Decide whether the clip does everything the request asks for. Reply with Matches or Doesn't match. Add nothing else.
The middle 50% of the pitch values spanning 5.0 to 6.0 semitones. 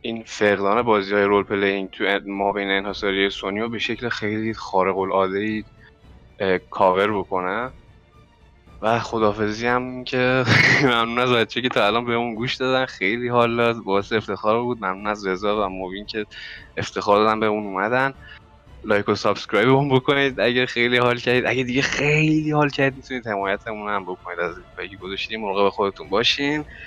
Doesn't match